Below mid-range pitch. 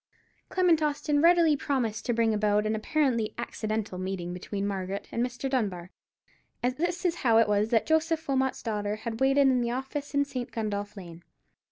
No: high, 235 Hz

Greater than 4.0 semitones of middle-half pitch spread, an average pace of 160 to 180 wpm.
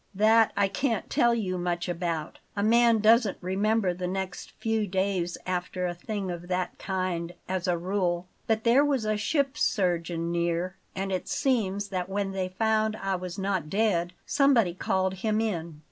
No: average, 3.4 semitones; average, 175 wpm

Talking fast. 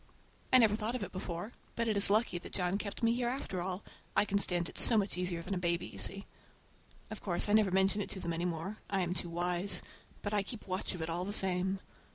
Yes: fast, 245 wpm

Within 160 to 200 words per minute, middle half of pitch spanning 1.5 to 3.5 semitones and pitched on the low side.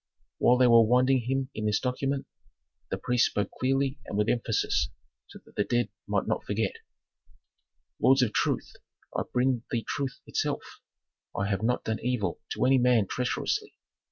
Yes: average, 165 wpm; average, 2.9 semitones; low, 125 Hz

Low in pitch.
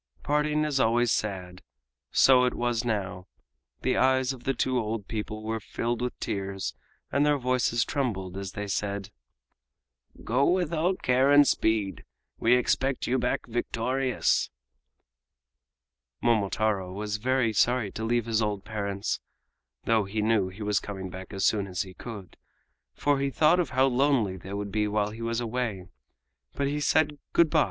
Yes: low, 115 Hz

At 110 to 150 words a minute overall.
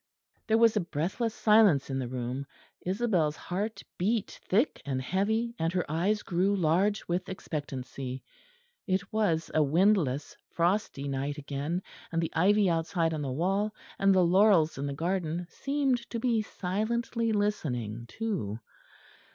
Yes: average, 145 wpm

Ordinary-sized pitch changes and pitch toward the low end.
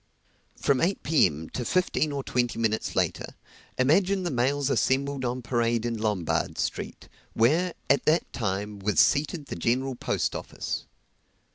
Yes: average, 4.0 semitones; low, 130 Hz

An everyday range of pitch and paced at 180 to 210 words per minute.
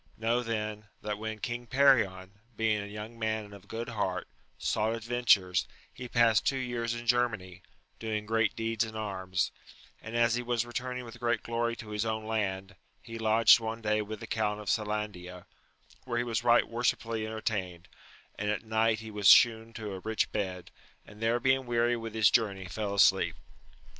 No: narrow, 2.0 semitones; average, 185 wpm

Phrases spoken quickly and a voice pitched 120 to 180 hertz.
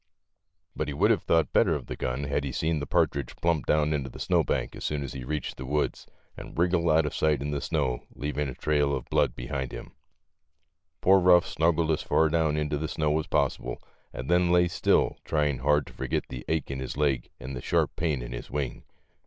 No: fast, 225 wpm; very low, 75 Hz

